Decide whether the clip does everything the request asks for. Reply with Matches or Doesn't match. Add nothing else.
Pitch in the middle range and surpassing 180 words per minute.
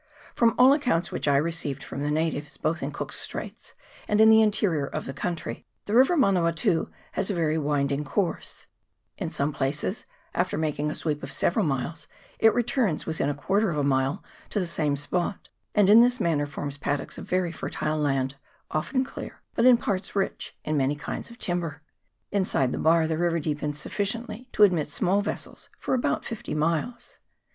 Matches